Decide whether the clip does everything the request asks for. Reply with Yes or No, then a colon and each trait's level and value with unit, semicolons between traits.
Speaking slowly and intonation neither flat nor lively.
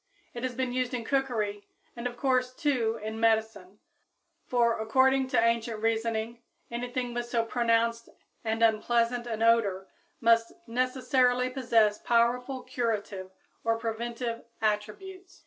No: slow, 130 wpm; narrow, 1.9 semitones